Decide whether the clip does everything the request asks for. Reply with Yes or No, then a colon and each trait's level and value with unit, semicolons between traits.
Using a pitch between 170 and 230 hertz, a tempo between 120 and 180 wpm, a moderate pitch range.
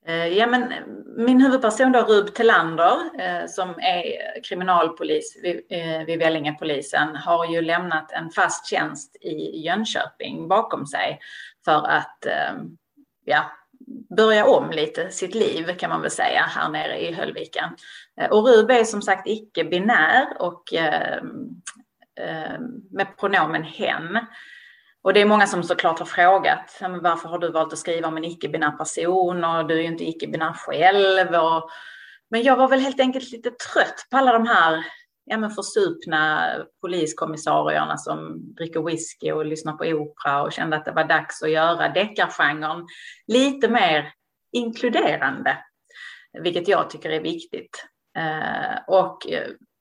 No: medium, 185 Hz; average, 145 wpm; wide, 7.0 semitones